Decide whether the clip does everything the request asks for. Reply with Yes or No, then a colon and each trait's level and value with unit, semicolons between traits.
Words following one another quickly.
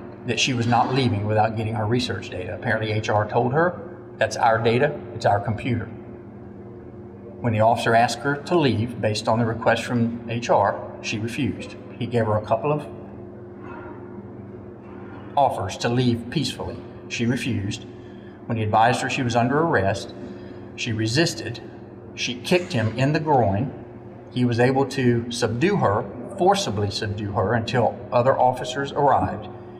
No: average, 155 wpm